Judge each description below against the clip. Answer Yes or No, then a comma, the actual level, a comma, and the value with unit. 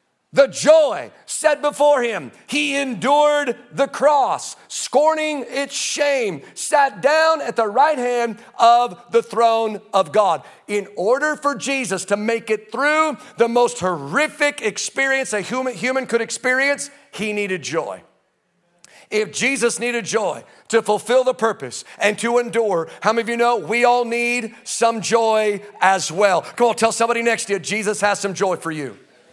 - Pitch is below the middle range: No, high, 235 Hz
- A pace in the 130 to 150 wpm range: No, average, 160 wpm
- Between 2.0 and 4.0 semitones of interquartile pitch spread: No, average, 4.6 semitones